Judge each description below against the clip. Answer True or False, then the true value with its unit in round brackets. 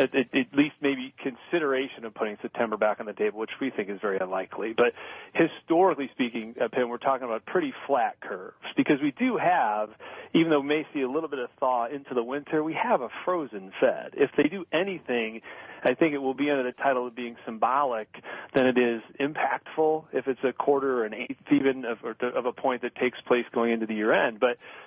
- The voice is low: True (130 Hz)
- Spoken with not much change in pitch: False (3.4 semitones)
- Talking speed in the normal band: False (210 wpm)